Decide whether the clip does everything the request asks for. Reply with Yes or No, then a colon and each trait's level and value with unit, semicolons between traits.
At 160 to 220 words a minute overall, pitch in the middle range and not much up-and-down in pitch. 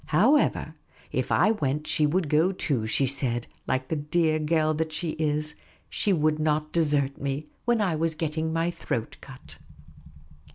Yes: average, 165 wpm; medium, 155 Hz; narrow, 2.2 semitones